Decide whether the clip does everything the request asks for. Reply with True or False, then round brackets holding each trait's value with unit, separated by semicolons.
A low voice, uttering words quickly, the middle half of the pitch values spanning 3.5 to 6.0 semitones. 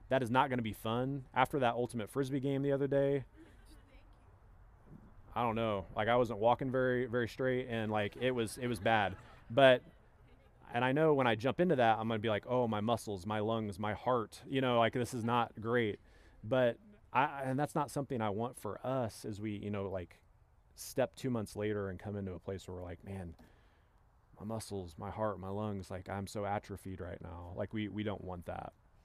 True (110 Hz; 220 wpm; 3.8 semitones)